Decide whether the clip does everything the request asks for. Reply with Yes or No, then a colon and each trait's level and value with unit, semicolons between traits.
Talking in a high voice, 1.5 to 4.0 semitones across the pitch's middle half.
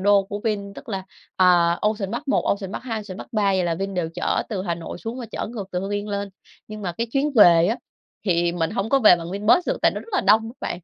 Yes: high, 200 Hz; average, 3.5 semitones